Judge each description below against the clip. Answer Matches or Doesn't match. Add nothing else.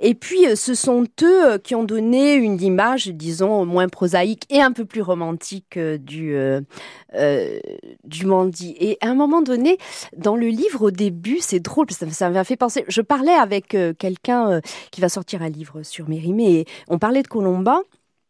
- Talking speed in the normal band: Matches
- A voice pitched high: Matches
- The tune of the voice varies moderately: Doesn't match